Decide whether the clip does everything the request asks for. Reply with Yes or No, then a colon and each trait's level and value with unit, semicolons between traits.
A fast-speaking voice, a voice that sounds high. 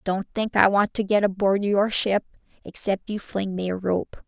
Yes: fast, 210 wpm; high, 200 Hz